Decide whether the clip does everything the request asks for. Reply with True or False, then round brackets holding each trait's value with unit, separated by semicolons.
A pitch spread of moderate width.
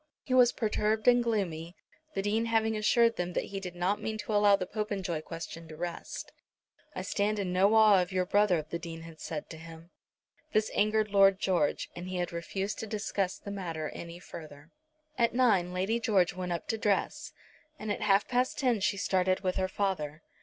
True (3.6 semitones)